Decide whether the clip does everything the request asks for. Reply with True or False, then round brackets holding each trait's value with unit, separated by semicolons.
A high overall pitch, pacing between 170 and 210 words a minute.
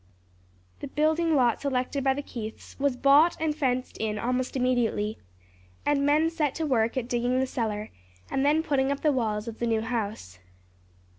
True (255 Hz; 175 wpm)